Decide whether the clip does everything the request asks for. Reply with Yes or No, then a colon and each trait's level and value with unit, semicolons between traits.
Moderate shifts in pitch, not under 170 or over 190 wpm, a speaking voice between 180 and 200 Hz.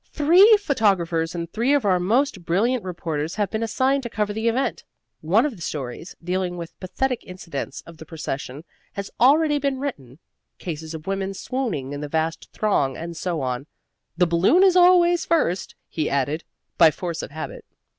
No: wide, 8.0 semitones; average, 175 wpm; medium, 185 Hz